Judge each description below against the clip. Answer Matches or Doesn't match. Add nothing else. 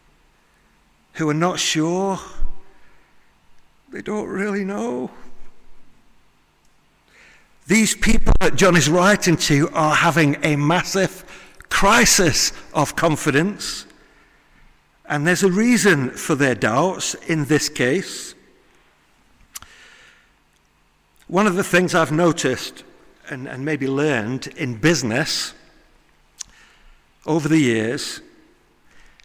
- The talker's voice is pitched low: Doesn't match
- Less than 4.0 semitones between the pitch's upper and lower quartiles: Doesn't match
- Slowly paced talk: Matches